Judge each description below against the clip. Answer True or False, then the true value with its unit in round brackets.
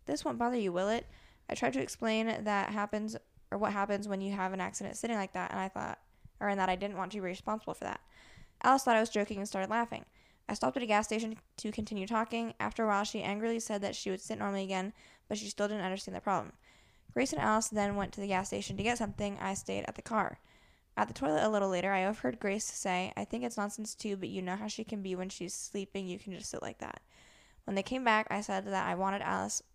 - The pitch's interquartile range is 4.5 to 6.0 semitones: False (2.4 semitones)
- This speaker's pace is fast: True (265 wpm)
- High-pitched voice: True (200 Hz)